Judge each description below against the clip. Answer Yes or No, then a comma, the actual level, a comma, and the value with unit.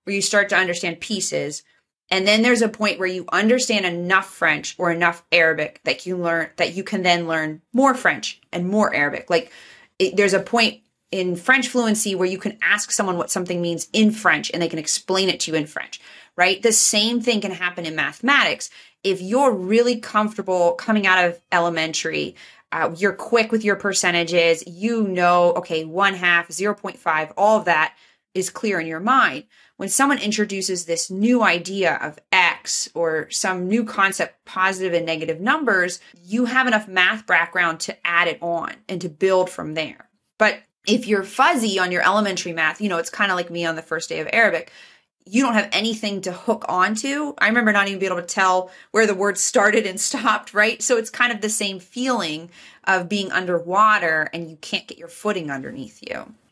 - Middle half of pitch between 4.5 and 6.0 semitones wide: No, average, 3.8 semitones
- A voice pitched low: No, high, 190 Hz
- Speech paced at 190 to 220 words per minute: Yes, average, 200 wpm